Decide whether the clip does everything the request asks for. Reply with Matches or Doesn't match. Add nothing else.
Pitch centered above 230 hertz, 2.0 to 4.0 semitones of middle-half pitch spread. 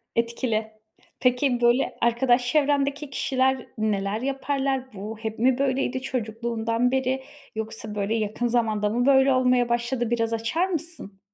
Matches